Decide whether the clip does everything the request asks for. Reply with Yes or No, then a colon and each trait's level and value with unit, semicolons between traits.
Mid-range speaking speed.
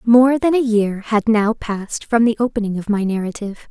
No: fast, 210 wpm